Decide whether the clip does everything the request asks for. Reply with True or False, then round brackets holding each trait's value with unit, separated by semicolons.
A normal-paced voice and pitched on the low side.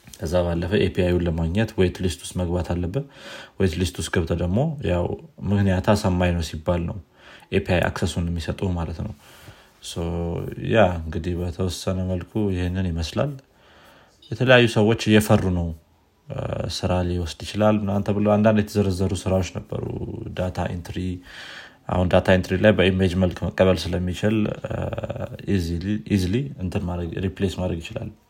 False (120 wpm; 95 Hz)